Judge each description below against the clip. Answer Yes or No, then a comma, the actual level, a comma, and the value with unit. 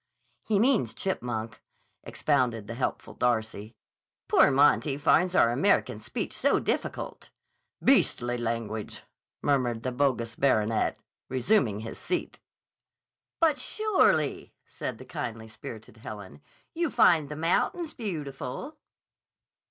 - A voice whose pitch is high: No, low, 130 Hz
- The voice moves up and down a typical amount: No, wide, 7.6 semitones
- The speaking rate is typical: No, slow, 110 wpm